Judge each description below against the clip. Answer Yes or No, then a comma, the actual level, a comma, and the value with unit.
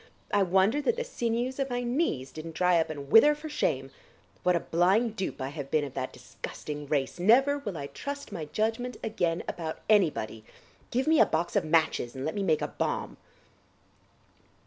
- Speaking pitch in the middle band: Yes, medium, 180 Hz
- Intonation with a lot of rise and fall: Yes, wide, 8.0 semitones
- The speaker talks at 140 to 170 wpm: No, average, 190 wpm